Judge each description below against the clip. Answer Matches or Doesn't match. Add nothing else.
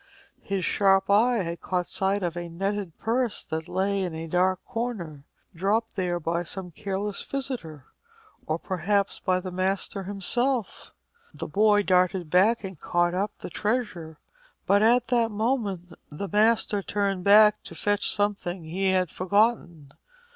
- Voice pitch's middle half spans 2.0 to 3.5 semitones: Matches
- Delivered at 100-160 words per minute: Matches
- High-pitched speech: Matches